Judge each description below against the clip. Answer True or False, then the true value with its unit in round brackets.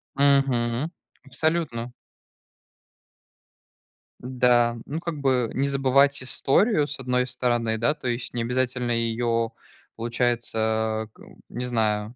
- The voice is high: False (125 Hz)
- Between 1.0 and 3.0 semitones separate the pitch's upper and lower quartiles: True (2.7 semitones)